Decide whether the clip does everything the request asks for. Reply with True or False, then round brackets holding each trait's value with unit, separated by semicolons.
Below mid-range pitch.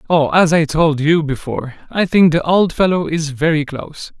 False (160 Hz)